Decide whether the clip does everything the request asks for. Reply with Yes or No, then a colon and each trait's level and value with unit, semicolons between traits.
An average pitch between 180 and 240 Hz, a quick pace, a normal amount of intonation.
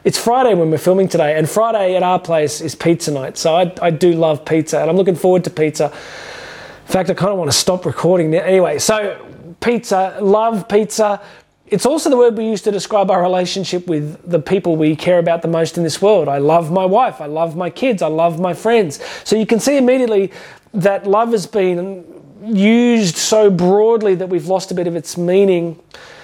Yes: medium, 185 Hz; fast, 215 wpm; average, 3.6 semitones